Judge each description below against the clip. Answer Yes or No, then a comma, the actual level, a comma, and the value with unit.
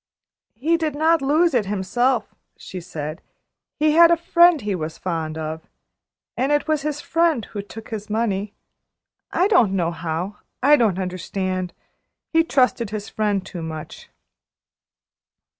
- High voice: Yes, high, 215 Hz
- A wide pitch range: Yes, wide, 8.3 semitones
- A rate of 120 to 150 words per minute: Yes, average, 145 wpm